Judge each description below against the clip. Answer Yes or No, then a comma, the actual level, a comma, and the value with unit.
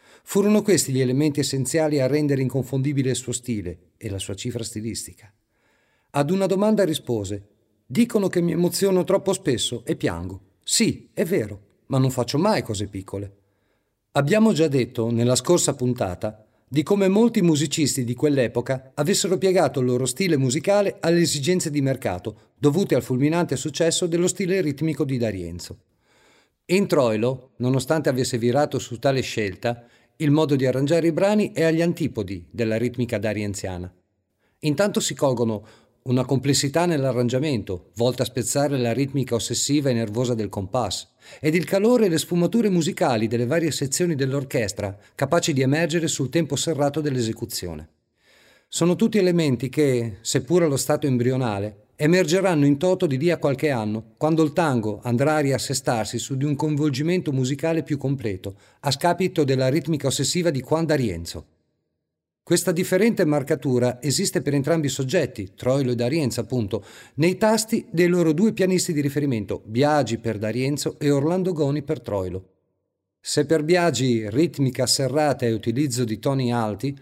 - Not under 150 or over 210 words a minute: Yes, average, 155 wpm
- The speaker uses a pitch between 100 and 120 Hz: No, low, 135 Hz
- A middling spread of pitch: No, wide, 5.7 semitones